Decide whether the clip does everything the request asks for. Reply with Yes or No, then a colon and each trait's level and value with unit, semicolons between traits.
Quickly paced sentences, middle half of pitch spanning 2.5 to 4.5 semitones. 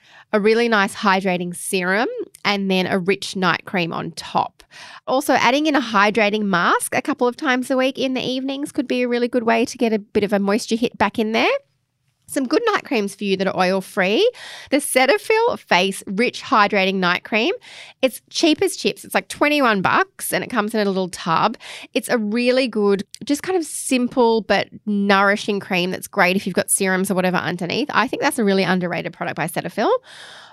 No: fast, 210 wpm; average, 5.2 semitones